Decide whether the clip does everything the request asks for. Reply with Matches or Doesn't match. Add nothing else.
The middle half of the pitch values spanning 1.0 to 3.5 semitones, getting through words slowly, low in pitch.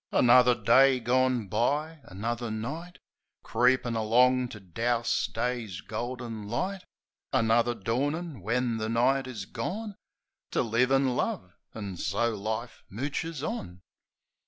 Matches